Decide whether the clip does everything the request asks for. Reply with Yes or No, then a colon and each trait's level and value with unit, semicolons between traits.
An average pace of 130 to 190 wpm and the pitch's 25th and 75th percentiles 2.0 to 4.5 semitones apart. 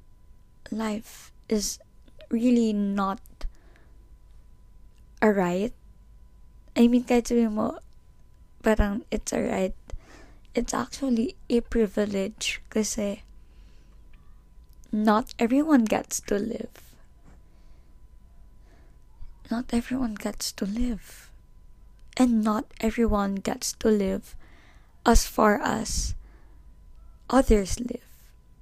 No: slow, 80 wpm; narrow, 2.4 semitones